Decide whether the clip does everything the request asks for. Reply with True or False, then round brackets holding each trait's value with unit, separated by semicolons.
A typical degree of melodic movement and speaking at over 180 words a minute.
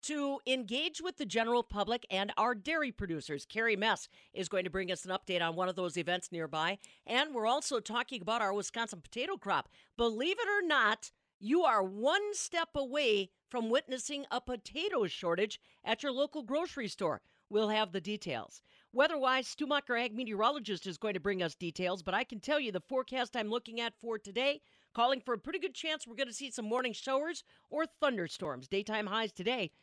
False (5.9 semitones; 195 wpm)